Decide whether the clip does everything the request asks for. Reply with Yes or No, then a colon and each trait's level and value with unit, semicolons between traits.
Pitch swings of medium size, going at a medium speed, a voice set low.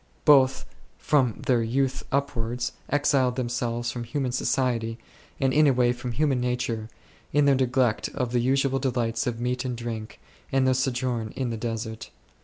No: narrow, 2.1 semitones; average, 170 wpm; low, 125 Hz